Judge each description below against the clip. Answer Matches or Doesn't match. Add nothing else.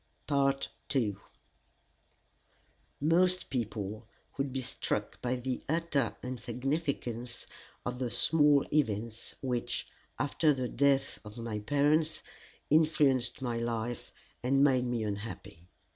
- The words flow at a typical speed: Doesn't match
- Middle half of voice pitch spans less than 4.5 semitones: Matches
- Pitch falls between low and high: Doesn't match